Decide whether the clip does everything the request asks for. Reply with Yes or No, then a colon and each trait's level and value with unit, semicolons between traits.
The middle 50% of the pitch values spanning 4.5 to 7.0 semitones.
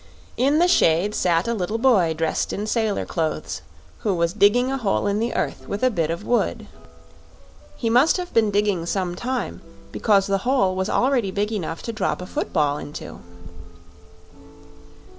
Yes: average, 4.9 semitones